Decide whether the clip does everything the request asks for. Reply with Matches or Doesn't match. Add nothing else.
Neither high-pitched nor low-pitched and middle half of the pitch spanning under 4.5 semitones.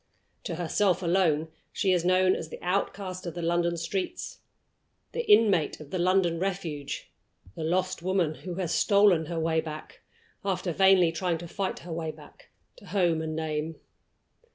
Matches